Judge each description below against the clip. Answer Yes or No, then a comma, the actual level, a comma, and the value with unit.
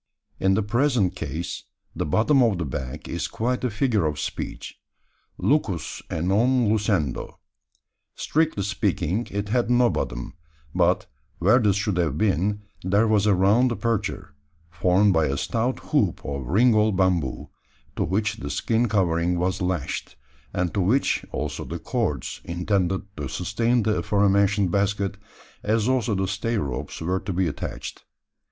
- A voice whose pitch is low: Yes, low, 100 Hz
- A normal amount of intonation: Yes, average, 3.9 semitones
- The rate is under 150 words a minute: No, average, 155 wpm